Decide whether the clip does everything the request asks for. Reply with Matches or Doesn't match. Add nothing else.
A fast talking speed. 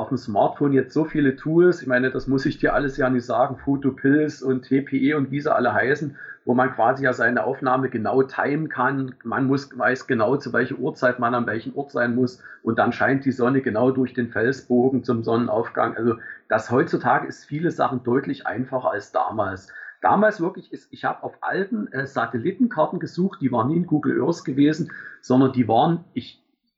Matches